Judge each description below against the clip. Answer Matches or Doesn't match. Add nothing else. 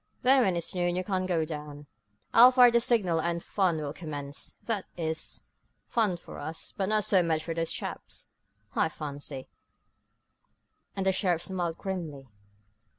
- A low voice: Doesn't match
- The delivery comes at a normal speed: Matches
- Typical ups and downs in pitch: Matches